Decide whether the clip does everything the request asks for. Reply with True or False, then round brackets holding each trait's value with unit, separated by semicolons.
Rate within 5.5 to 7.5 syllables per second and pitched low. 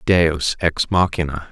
False (3.7 syllables/s; 80 Hz)